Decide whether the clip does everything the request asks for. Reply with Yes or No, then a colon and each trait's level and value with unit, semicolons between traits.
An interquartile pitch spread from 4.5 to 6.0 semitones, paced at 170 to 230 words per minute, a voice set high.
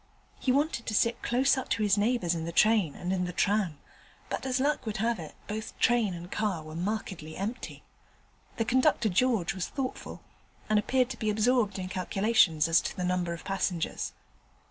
Yes: average, 4.8 semitones; average, 190 wpm; high, 210 Hz